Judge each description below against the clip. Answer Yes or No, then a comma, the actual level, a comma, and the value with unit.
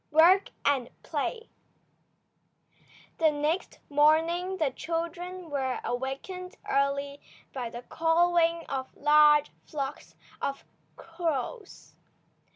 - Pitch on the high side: Yes, very high, 310 Hz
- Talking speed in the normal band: No, slow, 90 wpm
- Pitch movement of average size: Yes, average, 3.6 semitones